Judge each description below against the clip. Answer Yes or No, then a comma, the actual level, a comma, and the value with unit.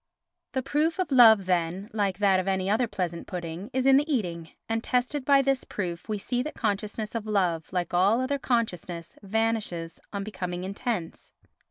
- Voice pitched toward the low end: No, high, 205 Hz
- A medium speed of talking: Yes, average, 180 wpm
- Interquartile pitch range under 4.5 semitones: No, average, 5.2 semitones